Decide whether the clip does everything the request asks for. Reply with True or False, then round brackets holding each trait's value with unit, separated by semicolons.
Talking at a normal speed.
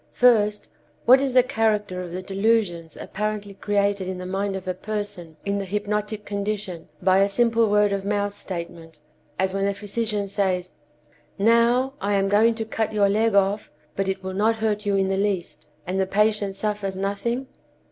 True (185 wpm)